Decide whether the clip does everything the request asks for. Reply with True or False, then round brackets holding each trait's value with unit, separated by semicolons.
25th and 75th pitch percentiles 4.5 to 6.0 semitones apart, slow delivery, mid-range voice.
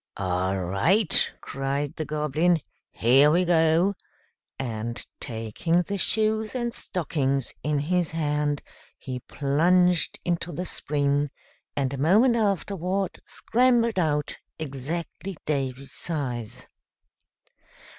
True (4.8 semitones; 105 wpm; 155 Hz)